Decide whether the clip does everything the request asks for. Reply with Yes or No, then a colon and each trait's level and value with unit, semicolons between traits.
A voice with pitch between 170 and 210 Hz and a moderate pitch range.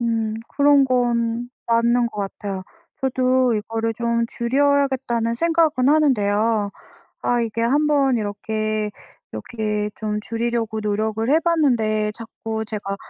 No: high, 230 Hz; average, 3.0 semitones